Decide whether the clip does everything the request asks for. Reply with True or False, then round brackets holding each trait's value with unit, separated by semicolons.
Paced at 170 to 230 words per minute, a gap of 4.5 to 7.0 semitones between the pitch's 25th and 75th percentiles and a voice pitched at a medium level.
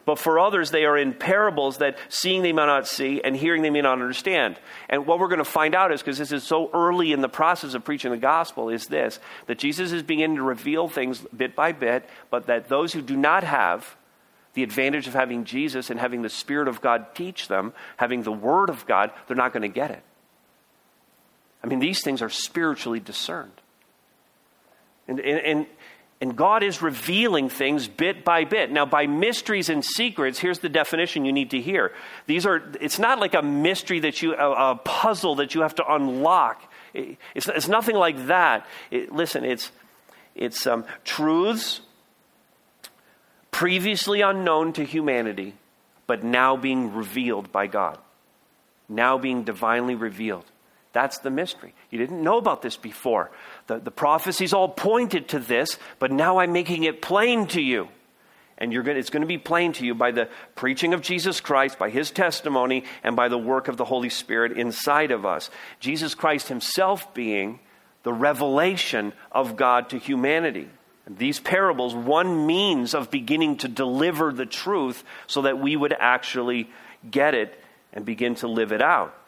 True (180 wpm; 5.4 semitones; 145 Hz)